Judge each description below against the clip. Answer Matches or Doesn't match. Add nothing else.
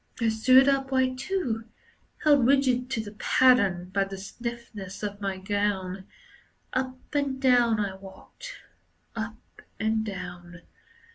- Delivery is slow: Matches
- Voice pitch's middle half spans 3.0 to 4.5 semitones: Doesn't match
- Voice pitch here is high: Matches